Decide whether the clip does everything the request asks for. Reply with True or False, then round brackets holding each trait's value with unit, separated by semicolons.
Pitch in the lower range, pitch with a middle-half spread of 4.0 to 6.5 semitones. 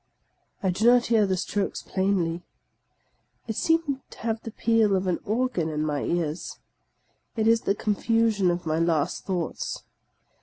False (200 Hz; 4.7 semitones)